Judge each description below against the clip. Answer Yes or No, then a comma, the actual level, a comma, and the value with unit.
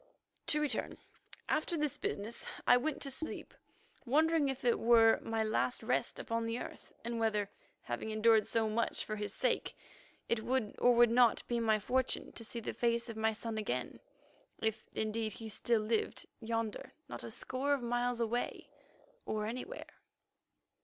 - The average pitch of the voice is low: No, high, 230 Hz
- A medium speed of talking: Yes, average, 165 wpm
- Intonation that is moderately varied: No, narrow, 2.1 semitones